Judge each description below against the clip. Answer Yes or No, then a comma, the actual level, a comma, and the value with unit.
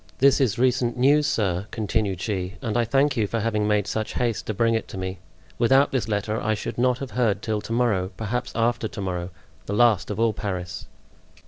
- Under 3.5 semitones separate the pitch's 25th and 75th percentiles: Yes, average, 3.0 semitones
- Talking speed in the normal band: No, fast, 210 wpm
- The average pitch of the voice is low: Yes, low, 110 Hz